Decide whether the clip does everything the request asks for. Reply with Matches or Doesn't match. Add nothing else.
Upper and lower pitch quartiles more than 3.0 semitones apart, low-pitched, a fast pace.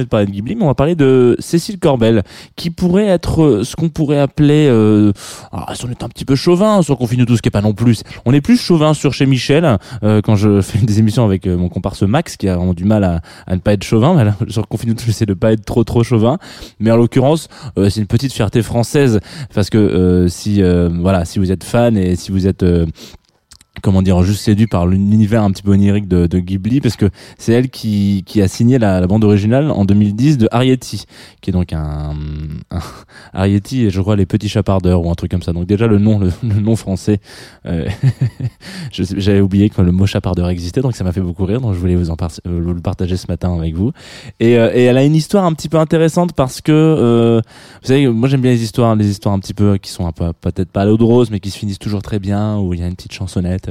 Matches